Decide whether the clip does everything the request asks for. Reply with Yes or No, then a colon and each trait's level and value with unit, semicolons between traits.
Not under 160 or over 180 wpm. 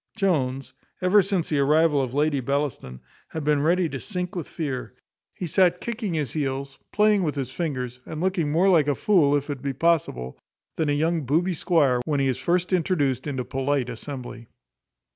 No: average, 190 wpm